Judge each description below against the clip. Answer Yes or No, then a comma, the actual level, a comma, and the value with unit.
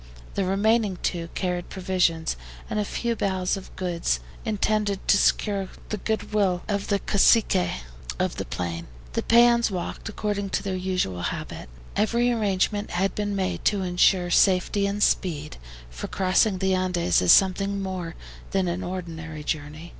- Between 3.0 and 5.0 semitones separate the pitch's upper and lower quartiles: No, narrow, 2.6 semitones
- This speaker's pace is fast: No, average, 155 wpm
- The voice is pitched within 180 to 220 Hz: Yes, high, 190 Hz